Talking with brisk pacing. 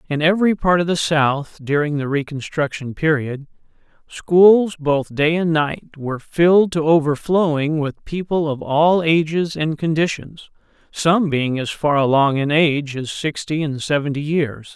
No: average, 155 wpm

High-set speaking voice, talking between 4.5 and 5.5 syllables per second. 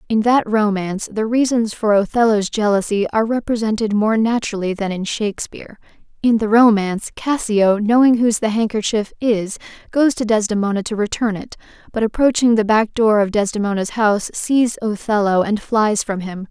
Yes: high, 215 Hz; 5.4 syllables/s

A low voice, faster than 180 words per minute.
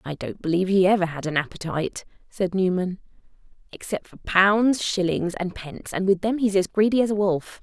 No: high, 190 Hz; average, 195 wpm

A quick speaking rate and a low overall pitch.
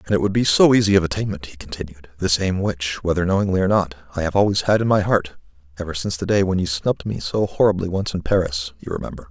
Yes: fast, 245 wpm; very low, 90 Hz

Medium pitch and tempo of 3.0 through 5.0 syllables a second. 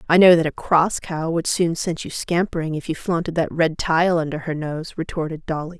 No: medium, 165 Hz; 5.2 syllables/s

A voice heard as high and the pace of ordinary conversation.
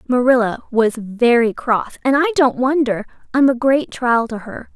Yes: very high, 250 Hz; average, 175 wpm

